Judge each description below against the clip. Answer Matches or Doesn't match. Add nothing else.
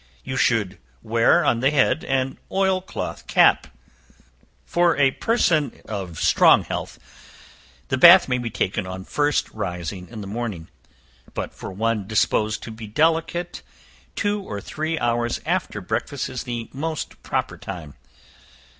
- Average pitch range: Doesn't match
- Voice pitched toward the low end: Matches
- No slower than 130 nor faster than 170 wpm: Matches